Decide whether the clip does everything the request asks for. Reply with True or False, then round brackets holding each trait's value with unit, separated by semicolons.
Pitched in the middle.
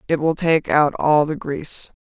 True (150 Hz)